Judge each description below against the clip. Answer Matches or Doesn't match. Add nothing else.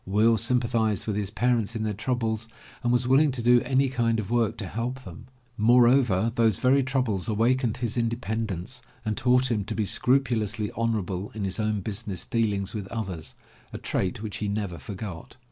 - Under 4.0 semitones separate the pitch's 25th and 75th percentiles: Matches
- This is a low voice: Matches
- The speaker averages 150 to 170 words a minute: Doesn't match